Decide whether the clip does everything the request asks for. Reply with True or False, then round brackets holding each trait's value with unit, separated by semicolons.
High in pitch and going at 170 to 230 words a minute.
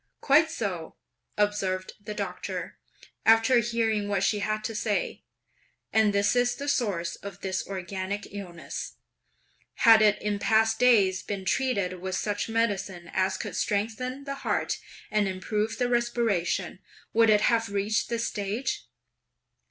False (210 Hz; 140 wpm)